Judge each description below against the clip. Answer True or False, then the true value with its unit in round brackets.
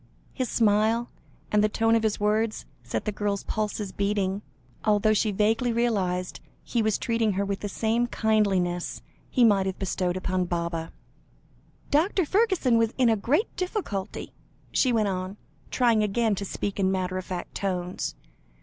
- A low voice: False (210 Hz)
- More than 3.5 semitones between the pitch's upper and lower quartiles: False (3.2 semitones)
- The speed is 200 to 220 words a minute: False (160 wpm)